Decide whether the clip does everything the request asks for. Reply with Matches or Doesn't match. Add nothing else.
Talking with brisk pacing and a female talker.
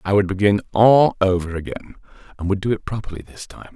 Doesn't match